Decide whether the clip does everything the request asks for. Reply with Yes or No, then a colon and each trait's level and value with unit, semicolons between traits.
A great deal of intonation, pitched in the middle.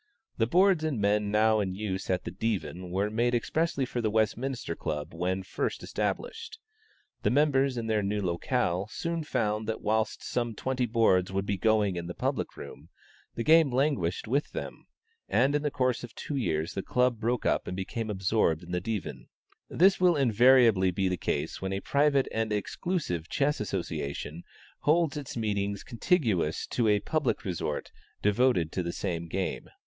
No: wide, 5.7 semitones; low, 110 Hz